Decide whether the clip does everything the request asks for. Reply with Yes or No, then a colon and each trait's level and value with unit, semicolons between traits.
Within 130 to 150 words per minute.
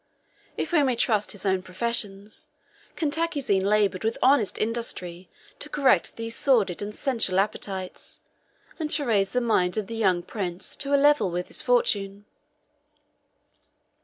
Yes: average, 145 wpm